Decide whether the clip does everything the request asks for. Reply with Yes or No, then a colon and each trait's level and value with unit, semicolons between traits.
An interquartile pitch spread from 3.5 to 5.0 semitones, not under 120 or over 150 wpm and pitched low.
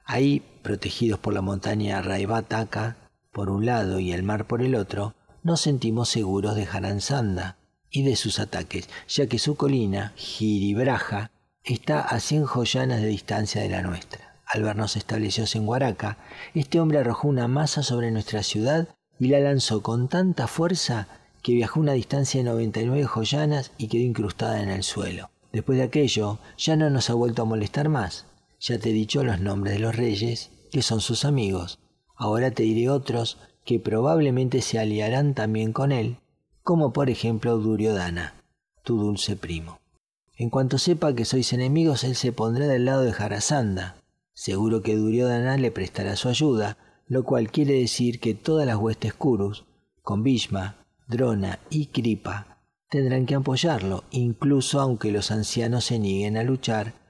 No: average, 4.0 semitones; average, 165 wpm; low, 115 Hz